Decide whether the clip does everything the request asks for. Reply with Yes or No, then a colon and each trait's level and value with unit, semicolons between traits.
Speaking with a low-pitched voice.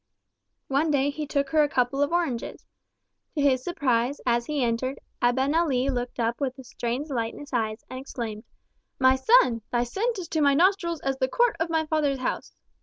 No: very high, 270 Hz